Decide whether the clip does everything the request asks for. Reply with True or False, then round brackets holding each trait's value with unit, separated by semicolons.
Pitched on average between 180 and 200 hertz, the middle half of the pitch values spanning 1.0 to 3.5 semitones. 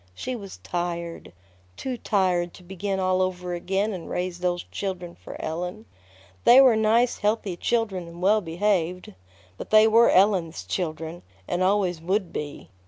True (185 Hz; 3.1 semitones)